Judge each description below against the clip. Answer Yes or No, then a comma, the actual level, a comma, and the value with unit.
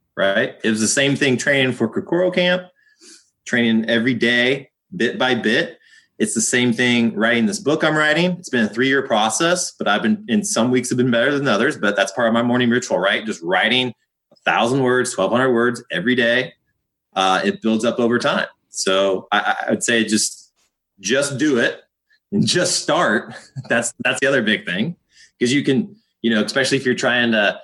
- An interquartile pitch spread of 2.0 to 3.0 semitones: No, average, 5.0 semitones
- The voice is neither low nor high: No, low, 125 Hz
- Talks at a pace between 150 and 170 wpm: No, average, 200 wpm